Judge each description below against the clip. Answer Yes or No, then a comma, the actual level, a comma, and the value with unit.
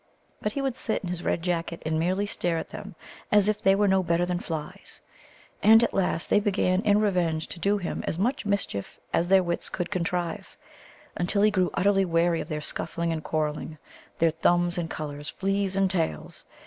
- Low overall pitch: No, medium, 180 Hz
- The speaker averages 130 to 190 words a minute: No, average, 200 wpm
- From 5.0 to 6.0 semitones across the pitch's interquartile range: No, average, 3.2 semitones